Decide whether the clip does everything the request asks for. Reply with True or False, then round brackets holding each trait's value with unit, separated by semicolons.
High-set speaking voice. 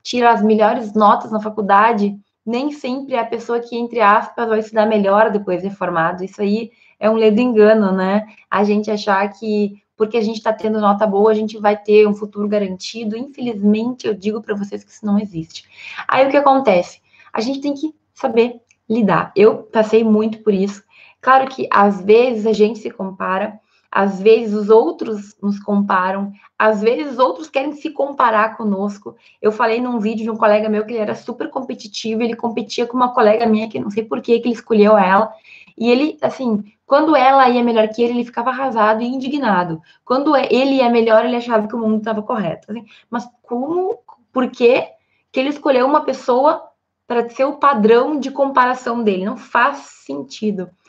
True (220 Hz)